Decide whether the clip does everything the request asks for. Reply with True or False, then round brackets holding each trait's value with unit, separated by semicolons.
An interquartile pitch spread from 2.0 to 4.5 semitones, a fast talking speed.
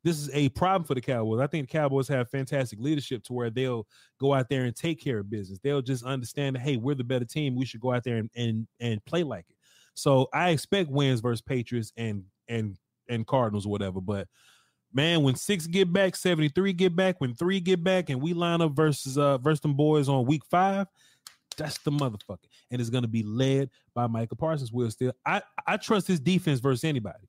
False (4.9 semitones; 230 wpm)